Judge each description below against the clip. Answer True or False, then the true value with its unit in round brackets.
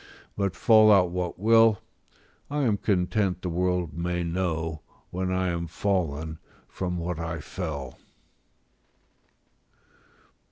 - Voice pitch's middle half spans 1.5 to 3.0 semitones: True (2.7 semitones)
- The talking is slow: True (115 wpm)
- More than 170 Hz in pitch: False (90 Hz)